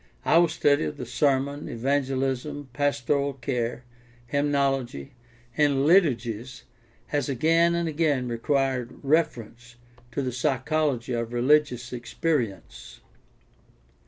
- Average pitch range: Yes, average, 3.2 semitones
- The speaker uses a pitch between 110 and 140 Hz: Yes, low, 135 Hz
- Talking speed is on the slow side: Yes, slow, 100 wpm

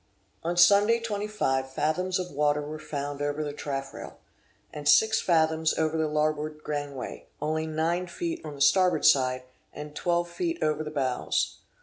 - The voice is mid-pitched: Yes, medium, 155 Hz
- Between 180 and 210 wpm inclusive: No, average, 155 wpm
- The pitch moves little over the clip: No, average, 3.2 semitones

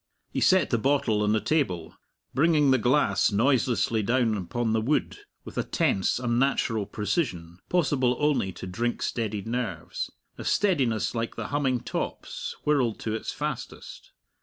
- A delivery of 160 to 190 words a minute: No, average, 150 wpm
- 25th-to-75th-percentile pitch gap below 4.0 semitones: No, average, 4.5 semitones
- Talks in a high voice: No, low, 120 Hz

